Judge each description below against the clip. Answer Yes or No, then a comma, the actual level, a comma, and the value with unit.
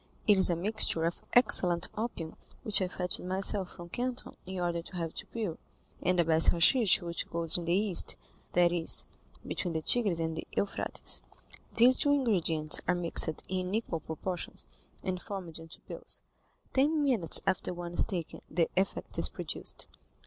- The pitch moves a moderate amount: Yes, average, 3.4 semitones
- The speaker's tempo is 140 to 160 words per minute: No, average, 170 wpm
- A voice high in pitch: No, medium, 180 Hz